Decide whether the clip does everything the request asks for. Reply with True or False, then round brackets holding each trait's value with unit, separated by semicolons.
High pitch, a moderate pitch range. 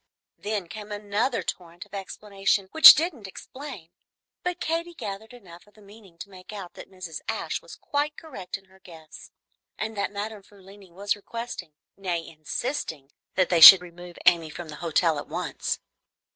True (195 Hz; 3.8 semitones)